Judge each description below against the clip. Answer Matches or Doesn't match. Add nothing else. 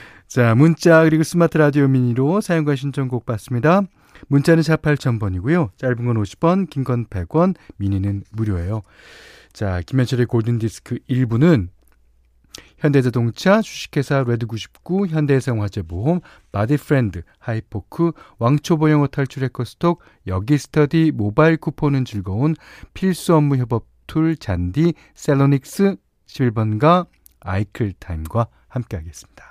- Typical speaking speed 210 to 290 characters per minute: Matches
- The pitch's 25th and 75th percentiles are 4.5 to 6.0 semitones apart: Doesn't match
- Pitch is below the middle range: Matches